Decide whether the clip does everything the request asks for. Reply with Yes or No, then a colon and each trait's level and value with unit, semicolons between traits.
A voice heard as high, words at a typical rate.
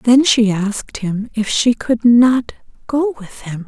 Yes: high, 230 Hz; average, 180 wpm